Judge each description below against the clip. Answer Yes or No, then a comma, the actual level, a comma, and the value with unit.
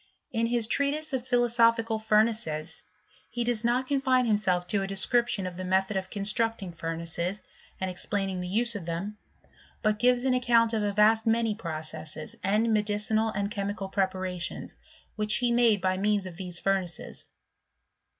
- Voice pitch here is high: Yes, high, 210 Hz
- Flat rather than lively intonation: No, average, 3.6 semitones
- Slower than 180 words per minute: Yes, average, 160 wpm